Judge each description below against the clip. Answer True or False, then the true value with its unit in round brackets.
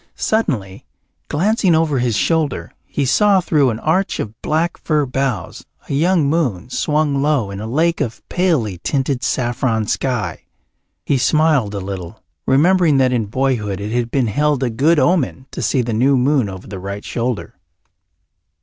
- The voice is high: False (130 Hz)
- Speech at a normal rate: True (165 wpm)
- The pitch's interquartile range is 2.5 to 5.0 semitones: False (5.6 semitones)